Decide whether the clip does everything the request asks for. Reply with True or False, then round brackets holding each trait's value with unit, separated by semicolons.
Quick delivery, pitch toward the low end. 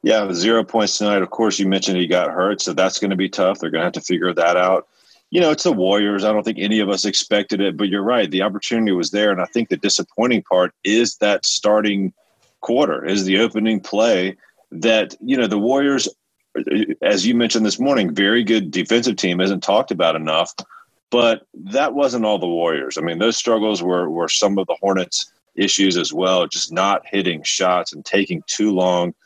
True (215 wpm; 100 Hz)